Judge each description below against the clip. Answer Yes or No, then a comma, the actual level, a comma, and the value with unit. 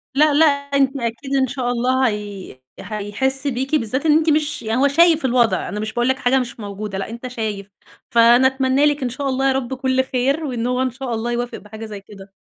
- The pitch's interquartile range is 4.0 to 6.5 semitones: No, average, 3.2 semitones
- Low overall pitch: No, very high, 255 Hz